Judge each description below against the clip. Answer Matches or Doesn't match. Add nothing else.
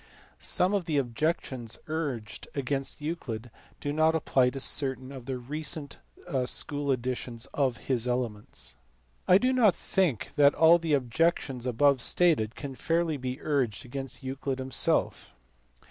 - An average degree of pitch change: Matches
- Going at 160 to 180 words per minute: Doesn't match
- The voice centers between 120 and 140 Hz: Matches